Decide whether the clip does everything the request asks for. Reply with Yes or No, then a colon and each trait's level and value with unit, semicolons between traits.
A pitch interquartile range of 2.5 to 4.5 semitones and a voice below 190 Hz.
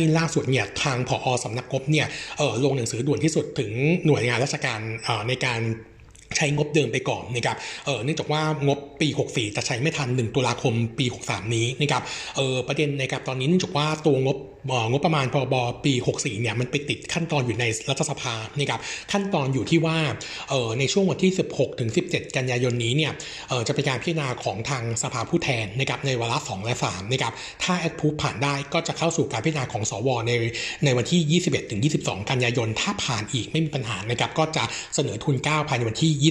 Yes: average, 3.9 semitones; low, 135 Hz